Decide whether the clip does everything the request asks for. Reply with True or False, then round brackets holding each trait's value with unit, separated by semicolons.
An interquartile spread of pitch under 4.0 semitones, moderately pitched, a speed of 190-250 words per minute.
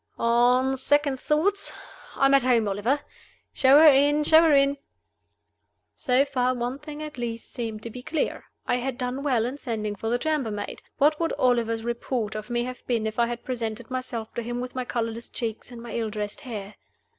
False (3.2 semitones; 245 Hz; 200 wpm)